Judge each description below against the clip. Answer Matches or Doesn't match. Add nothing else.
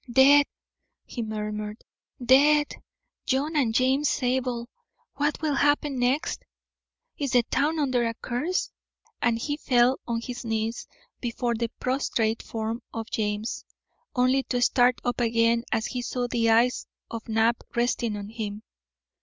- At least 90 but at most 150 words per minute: Matches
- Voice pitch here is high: Matches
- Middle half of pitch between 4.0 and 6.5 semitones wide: Doesn't match